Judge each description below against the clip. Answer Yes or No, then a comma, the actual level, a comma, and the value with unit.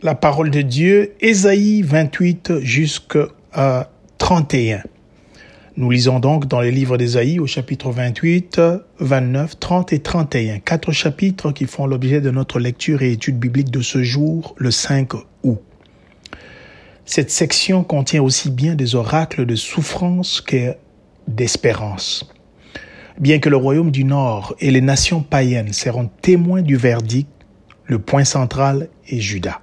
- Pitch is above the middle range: No, low, 135 Hz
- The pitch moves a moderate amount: Yes, average, 4.3 semitones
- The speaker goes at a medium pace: No, slow, 140 wpm